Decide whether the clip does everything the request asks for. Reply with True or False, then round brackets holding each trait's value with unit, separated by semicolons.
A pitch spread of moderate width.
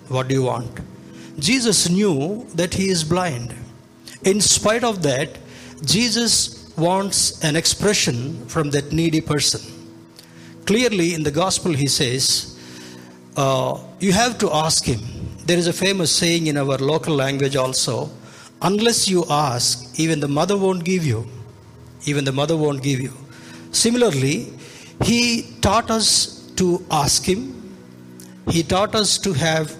False (6.7 semitones)